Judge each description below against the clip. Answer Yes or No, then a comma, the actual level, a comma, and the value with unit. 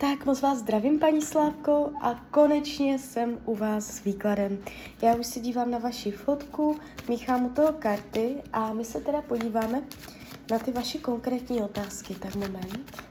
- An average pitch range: Yes, average, 4.4 semitones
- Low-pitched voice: No, high, 245 Hz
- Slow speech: No, average, 165 wpm